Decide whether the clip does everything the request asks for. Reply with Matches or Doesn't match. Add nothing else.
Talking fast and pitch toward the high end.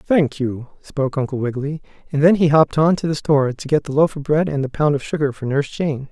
Doesn't match